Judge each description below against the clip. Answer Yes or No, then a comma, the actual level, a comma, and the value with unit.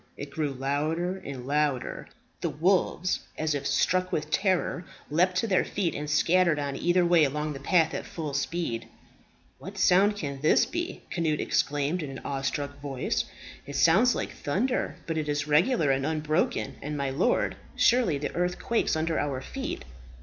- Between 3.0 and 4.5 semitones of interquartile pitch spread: Yes, average, 4.0 semitones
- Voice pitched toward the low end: No, medium, 155 Hz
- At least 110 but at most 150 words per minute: No, average, 170 wpm